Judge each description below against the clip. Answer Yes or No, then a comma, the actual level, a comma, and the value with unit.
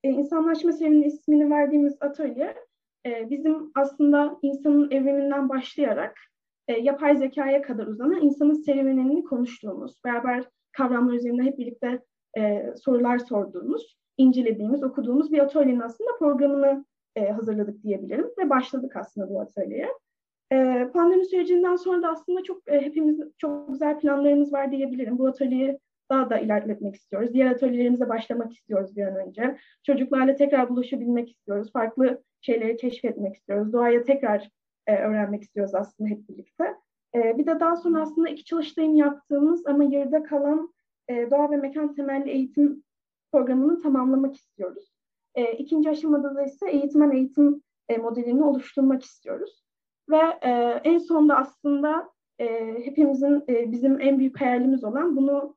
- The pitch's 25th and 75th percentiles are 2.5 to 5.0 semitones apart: Yes, average, 3.4 semitones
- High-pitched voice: Yes, very high, 275 Hz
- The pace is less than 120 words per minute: No, average, 125 wpm